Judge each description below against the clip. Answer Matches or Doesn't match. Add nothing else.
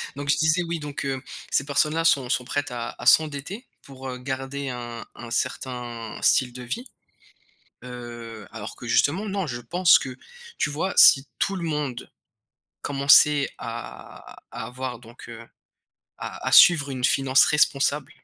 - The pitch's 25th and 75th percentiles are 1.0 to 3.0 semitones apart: Doesn't match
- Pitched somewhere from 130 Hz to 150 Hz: Matches